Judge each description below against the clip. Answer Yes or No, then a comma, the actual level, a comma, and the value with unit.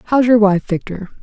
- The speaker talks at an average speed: Yes, average, 195 wpm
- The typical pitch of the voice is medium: No, high, 210 Hz